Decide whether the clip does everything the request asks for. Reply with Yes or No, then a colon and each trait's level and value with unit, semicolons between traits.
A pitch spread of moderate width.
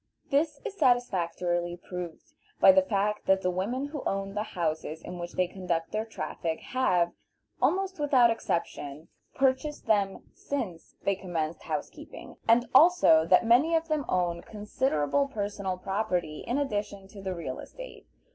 No: wide, 7.0 semitones